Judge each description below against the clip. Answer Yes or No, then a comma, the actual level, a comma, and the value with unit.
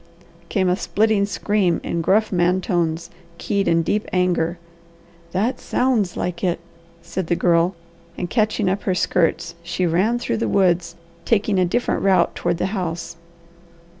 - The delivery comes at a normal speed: Yes, average, 155 wpm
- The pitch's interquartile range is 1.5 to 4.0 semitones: Yes, average, 2.9 semitones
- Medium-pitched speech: Yes, medium, 180 Hz